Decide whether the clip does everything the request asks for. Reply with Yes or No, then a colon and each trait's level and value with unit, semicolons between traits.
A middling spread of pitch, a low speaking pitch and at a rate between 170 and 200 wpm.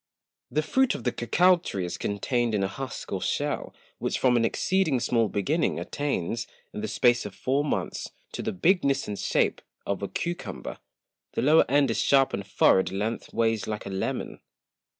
No: wide, 5.9 semitones; low, 120 Hz; average, 185 wpm